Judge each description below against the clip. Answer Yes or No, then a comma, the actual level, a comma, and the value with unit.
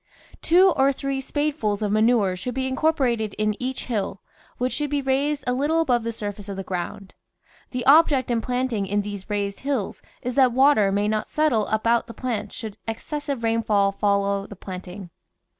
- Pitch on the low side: No, high, 230 Hz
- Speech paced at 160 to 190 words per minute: Yes, average, 180 wpm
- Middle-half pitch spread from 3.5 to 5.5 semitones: Yes, average, 4.7 semitones